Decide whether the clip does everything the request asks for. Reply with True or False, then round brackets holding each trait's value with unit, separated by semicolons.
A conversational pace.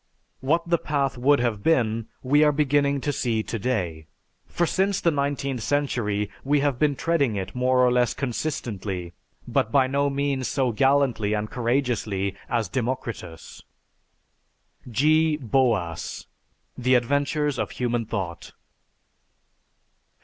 False (130 wpm)